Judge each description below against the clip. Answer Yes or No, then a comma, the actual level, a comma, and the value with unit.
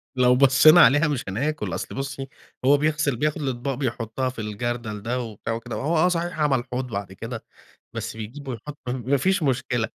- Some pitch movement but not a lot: Yes, average, 3.9 semitones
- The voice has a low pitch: Yes, low, 130 Hz